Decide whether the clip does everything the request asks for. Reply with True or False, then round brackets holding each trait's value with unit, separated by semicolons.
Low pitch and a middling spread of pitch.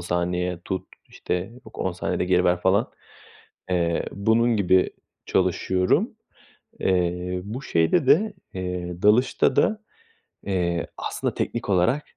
True (90 Hz; 3.3 semitones)